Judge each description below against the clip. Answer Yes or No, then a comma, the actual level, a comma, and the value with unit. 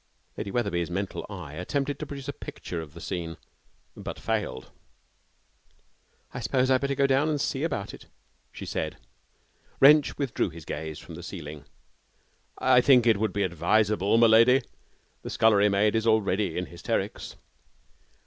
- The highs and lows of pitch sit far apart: Yes, wide, 7.0 semitones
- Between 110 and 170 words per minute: Yes, average, 160 wpm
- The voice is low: Yes, low, 105 Hz